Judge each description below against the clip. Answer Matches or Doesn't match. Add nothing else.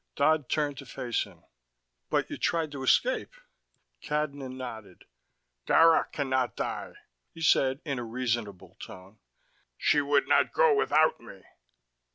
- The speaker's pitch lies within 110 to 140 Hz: Matches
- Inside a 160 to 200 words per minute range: Doesn't match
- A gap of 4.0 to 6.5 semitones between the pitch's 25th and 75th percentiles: Matches